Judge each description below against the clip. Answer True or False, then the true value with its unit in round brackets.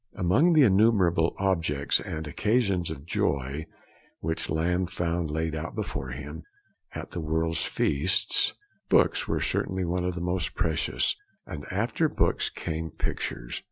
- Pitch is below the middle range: True (85 Hz)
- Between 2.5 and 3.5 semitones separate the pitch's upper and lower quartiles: True (3.1 semitones)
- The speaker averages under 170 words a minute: True (140 wpm)